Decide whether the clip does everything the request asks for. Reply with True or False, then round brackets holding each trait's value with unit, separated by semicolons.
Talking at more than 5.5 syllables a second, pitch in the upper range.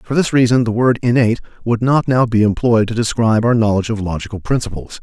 False (6.4 syllables/s; 115 Hz)